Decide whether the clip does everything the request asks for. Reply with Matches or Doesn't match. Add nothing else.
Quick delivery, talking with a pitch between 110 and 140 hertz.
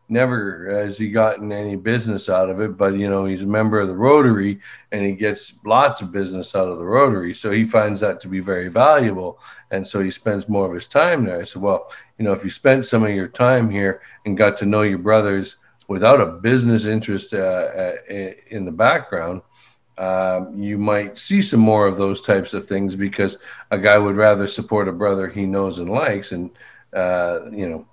Doesn't match